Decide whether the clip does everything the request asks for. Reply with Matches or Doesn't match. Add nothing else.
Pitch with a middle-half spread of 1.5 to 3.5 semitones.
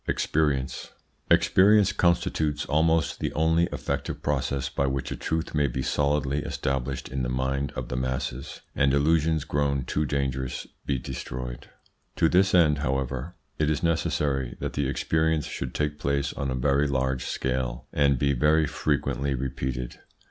Matches